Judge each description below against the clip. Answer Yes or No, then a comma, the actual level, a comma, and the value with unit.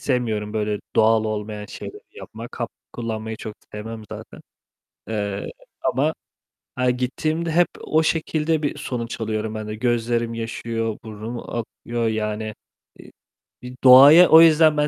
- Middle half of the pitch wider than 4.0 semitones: No, average, 3.0 semitones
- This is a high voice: No, low, 115 Hz